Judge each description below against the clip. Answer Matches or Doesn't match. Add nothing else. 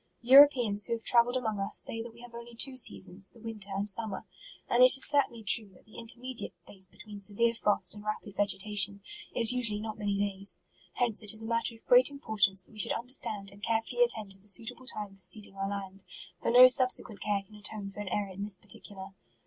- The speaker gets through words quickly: Matches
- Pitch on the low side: Doesn't match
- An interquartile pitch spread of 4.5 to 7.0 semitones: Doesn't match